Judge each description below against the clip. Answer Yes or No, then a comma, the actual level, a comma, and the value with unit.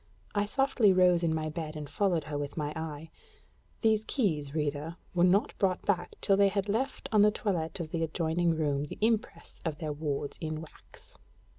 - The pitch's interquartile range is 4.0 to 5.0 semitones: Yes, average, 4.6 semitones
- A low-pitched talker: No, medium, 165 Hz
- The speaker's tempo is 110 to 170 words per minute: No, average, 190 wpm